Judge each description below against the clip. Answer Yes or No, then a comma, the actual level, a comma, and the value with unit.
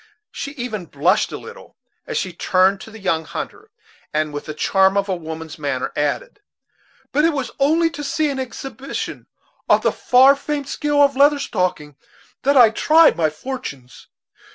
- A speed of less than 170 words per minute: No, average, 175 wpm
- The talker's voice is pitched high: Yes, high, 225 Hz